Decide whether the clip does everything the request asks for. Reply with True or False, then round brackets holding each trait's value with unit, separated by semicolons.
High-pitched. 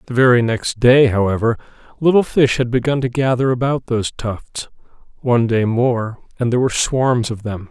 False (120 Hz)